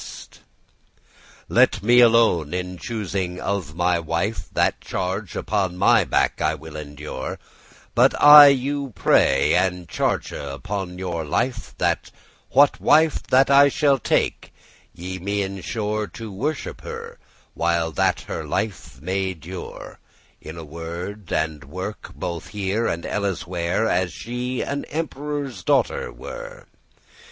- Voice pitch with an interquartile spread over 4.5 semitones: Yes, wide, 5.4 semitones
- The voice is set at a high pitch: No, very low, 95 Hz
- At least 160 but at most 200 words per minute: No, slow, 135 wpm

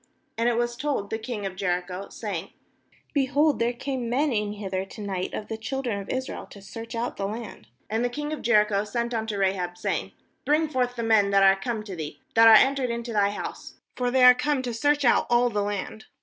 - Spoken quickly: Yes, fast, 235 wpm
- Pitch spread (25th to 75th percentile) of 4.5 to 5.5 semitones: No, average, 3.7 semitones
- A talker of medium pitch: No, high, 225 Hz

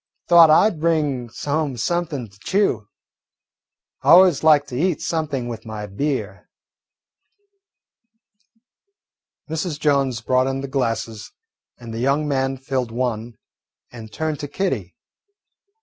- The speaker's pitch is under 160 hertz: Yes, low, 135 Hz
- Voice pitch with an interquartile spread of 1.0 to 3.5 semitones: No, average, 4.9 semitones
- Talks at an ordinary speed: No, slow, 125 wpm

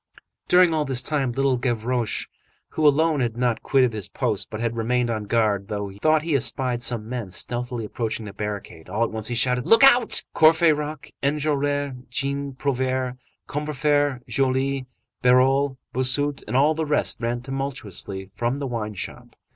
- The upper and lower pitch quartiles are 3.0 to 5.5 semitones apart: Yes, average, 3.5 semitones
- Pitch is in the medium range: No, low, 130 Hz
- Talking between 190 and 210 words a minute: No, average, 160 wpm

